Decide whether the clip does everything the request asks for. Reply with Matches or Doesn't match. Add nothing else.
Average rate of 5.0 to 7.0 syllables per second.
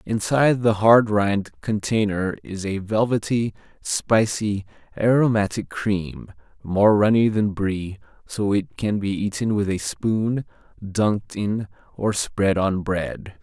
Doesn't match